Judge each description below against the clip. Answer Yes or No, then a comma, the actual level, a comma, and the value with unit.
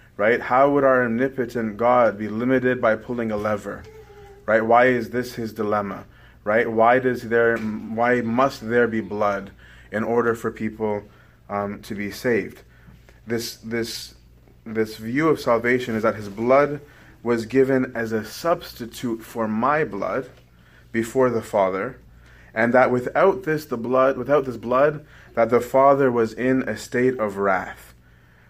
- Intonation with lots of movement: No, average, 2.9 semitones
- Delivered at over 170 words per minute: No, average, 155 wpm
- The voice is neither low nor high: No, low, 115 Hz